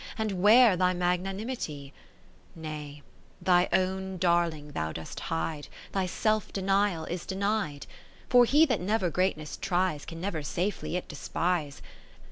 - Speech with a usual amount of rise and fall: Yes, average, 3.8 semitones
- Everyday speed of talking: No, slow, 130 wpm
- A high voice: No, medium, 180 Hz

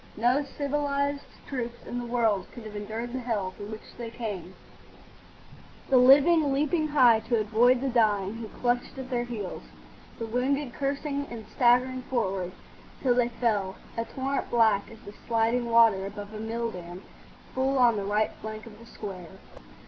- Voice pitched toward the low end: No, high, 235 Hz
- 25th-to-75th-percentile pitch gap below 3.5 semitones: Yes, average, 3.1 semitones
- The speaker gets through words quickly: No, average, 165 wpm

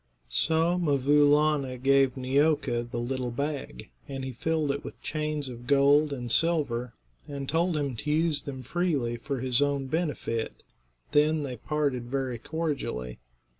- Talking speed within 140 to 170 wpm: Yes, average, 150 wpm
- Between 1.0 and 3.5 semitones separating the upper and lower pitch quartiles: Yes, average, 3.1 semitones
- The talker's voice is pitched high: No, medium, 140 Hz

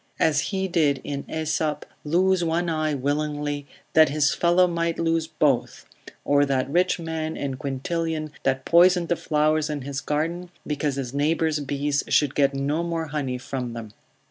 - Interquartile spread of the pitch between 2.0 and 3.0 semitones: Yes, average, 2.7 semitones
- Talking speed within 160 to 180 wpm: Yes, average, 165 wpm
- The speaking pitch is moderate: Yes, medium, 150 Hz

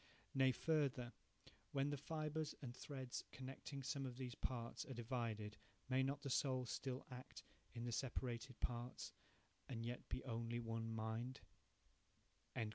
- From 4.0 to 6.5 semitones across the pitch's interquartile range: No, narrow, 2.4 semitones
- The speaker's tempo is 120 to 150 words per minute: Yes, average, 140 wpm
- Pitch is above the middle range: No, low, 125 Hz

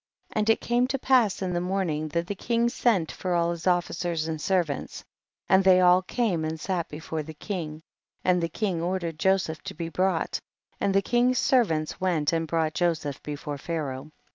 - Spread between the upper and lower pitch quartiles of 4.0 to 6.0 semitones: No, average, 3.3 semitones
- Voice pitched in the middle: Yes, medium, 175 Hz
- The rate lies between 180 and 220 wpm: Yes, average, 190 wpm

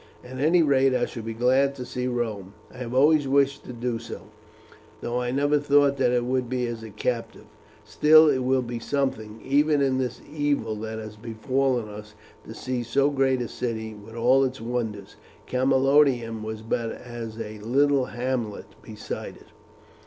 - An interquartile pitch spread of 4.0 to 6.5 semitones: No, average, 3.1 semitones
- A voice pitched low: Yes, low, 125 Hz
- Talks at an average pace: Yes, average, 180 wpm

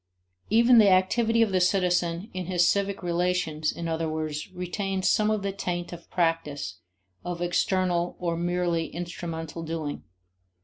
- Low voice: No, medium, 175 Hz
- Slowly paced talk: No, average, 145 wpm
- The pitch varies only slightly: Yes, narrow, 2.3 semitones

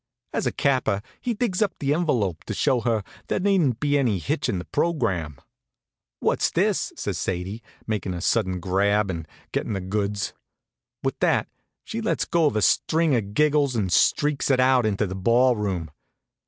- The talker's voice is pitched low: Yes, low, 110 Hz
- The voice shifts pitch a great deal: Yes, wide, 6.9 semitones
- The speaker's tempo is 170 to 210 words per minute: Yes, average, 175 wpm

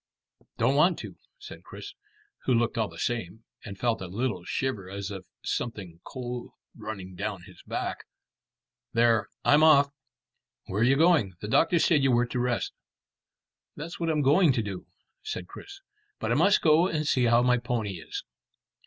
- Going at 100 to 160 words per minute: No, average, 175 wpm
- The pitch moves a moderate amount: No, wide, 6.0 semitones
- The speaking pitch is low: Yes, low, 120 Hz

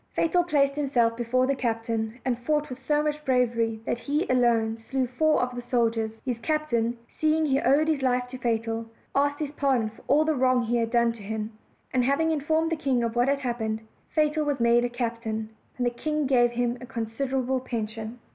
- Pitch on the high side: Yes, very high, 250 Hz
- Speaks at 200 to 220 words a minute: Yes, fast, 205 wpm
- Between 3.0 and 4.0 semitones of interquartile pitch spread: Yes, average, 3.4 semitones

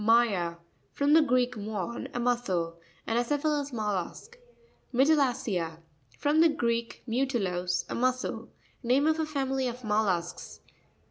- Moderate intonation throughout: No, wide, 6.3 semitones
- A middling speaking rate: No, slow, 120 wpm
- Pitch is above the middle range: Yes, high, 240 Hz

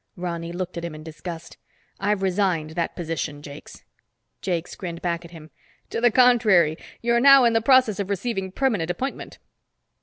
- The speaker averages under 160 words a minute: No, average, 170 wpm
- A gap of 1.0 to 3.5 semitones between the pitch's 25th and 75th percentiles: No, average, 5.2 semitones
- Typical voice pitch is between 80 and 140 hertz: No, medium, 180 Hz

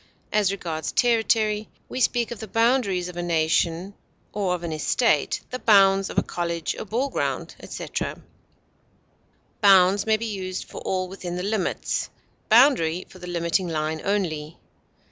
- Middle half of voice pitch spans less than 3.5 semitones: No, average, 3.9 semitones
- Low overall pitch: No, high, 190 Hz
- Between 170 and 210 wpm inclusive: No, average, 155 wpm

